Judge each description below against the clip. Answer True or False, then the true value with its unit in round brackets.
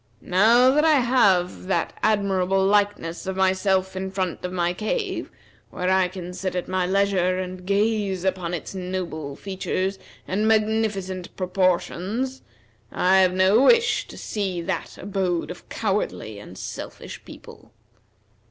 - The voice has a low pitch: False (190 Hz)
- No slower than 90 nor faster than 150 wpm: True (140 wpm)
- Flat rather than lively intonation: True (2.1 semitones)